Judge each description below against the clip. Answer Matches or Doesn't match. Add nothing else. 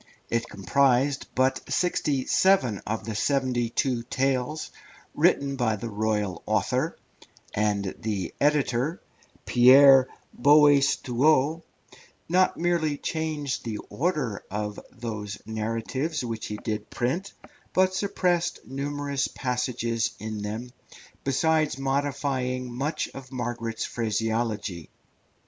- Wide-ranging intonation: Doesn't match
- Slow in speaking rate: Matches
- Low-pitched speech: Matches